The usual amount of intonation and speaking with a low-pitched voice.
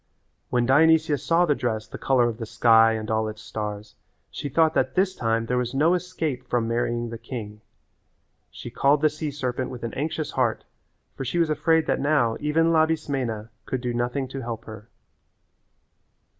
Yes: average, 5.0 semitones; low, 125 Hz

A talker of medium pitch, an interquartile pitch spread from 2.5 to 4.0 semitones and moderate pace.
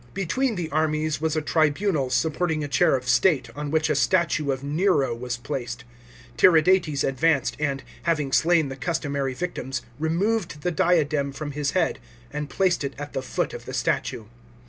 Yes: medium, 150 Hz; average, 3.6 semitones; average, 170 wpm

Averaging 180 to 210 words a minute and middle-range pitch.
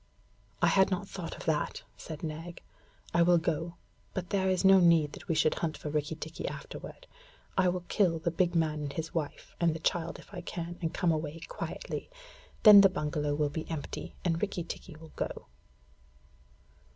Yes: average, 190 wpm; medium, 165 Hz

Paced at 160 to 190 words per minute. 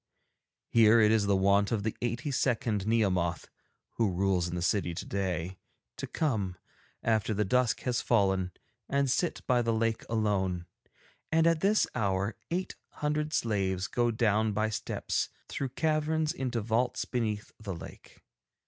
No: average, 150 wpm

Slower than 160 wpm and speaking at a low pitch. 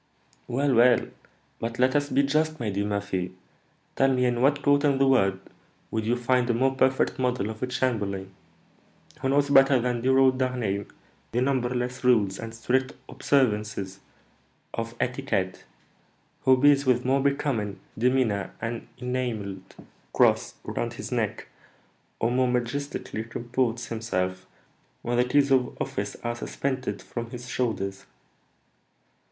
Yes: average, 145 wpm; low, 125 Hz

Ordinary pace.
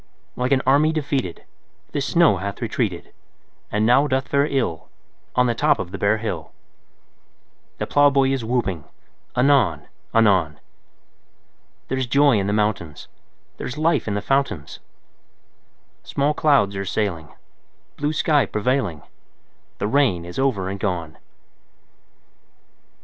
No: slow, 130 wpm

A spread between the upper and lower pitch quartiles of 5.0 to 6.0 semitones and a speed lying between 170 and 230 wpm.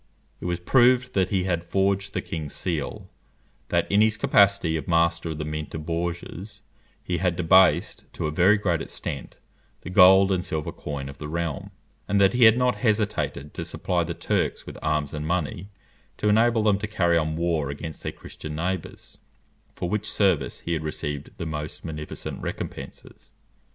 No: average, 4.2 semitones; average, 180 wpm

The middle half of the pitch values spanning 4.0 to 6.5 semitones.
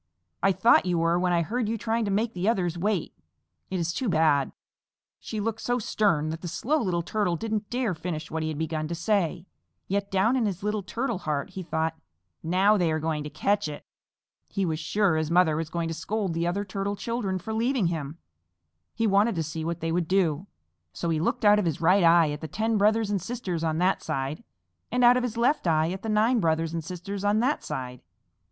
Yes: average, 4.7 semitones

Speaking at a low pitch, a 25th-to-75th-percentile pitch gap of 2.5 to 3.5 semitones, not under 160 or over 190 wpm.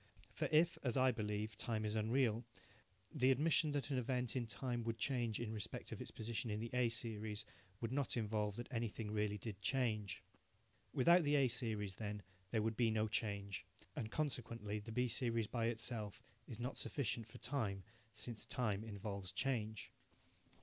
Yes: low, 115 Hz; average, 2.8 semitones; average, 175 wpm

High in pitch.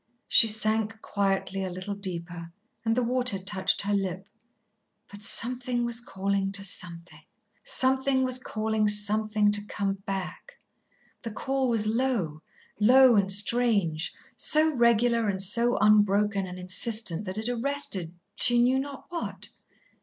Yes: high, 210 Hz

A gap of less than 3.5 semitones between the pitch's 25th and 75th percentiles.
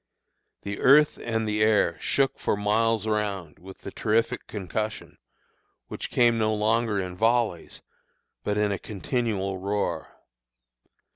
Yes: narrow, 2.5 semitones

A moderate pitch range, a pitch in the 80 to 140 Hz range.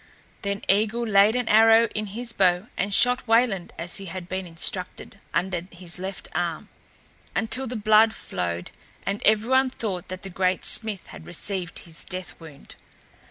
No: average, 3.7 semitones; high, 195 Hz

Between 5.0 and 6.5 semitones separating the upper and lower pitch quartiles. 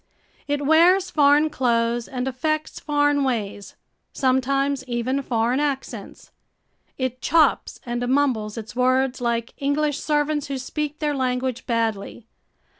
No: average, 3.2 semitones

